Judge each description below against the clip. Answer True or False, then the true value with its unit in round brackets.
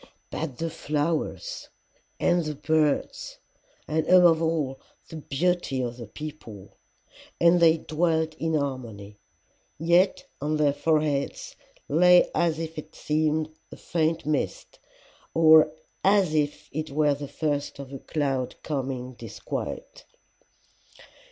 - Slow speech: True (120 wpm)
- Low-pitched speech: False (155 Hz)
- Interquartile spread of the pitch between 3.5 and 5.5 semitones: False (2.6 semitones)